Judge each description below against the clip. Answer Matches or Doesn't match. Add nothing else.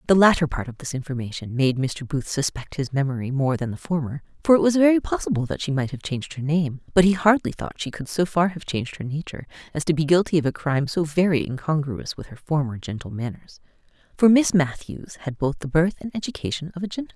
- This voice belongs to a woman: Matches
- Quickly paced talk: Matches